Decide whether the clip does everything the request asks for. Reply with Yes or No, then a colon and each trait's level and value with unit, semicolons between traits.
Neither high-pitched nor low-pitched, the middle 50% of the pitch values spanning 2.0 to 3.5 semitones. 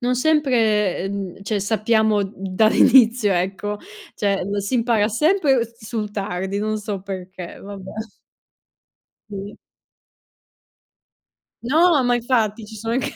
No: high, 215 Hz; average, 3.1 semitones